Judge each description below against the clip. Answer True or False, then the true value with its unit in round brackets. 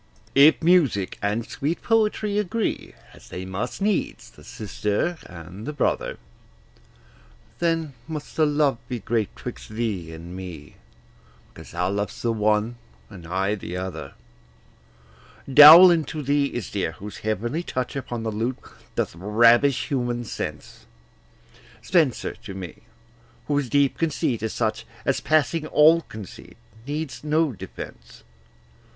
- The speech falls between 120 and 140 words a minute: True (135 wpm)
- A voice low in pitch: True (120 Hz)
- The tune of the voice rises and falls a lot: True (6.9 semitones)